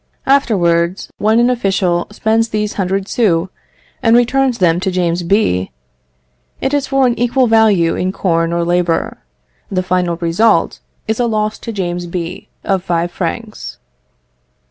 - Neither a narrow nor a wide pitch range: Yes, average, 4.6 semitones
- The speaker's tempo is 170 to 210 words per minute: No, average, 145 wpm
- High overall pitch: Yes, high, 195 Hz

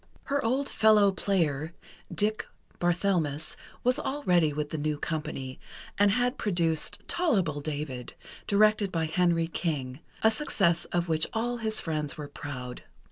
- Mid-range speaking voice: Yes, medium, 170 Hz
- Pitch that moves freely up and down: Yes, wide, 5.9 semitones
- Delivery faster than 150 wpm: No, slow, 135 wpm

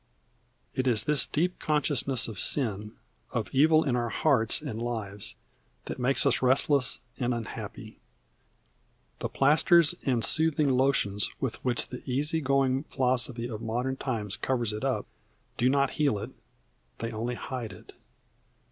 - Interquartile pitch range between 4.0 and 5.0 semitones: No, average, 3.3 semitones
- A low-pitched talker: Yes, low, 130 Hz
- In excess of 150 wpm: No, average, 145 wpm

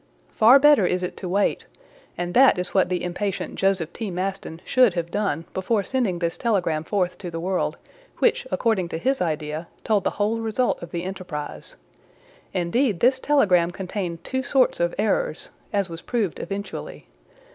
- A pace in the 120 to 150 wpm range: No, average, 170 wpm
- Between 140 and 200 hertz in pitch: Yes, high, 190 Hz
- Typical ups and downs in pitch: Yes, average, 4.6 semitones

